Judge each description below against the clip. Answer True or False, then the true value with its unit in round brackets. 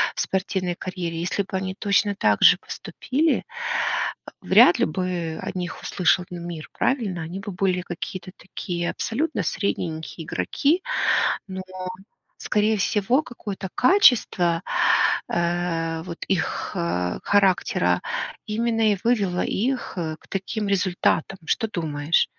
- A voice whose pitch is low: False (185 Hz)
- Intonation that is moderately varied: True (3.4 semitones)